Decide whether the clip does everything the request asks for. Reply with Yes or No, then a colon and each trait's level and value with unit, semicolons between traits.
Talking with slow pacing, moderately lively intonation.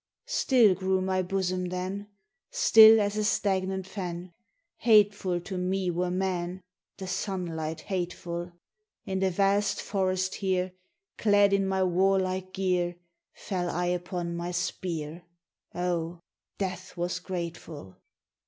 No: slow, 125 wpm; narrow, 1.5 semitones